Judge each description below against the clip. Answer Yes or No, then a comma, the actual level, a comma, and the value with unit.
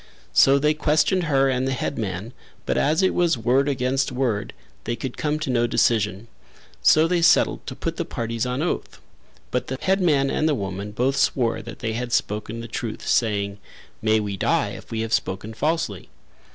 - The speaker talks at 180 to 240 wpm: Yes, average, 190 wpm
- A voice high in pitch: No, low, 125 Hz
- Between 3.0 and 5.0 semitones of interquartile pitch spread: Yes, average, 4.6 semitones